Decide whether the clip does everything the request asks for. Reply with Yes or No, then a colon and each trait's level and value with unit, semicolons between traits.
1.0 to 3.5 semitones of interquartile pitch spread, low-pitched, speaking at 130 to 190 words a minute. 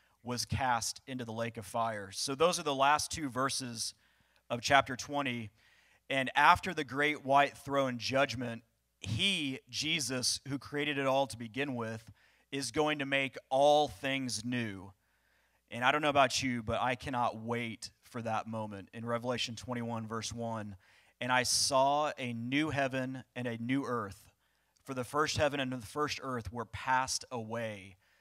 Yes: average, 3.2 semitones; low, 125 Hz; average, 170 wpm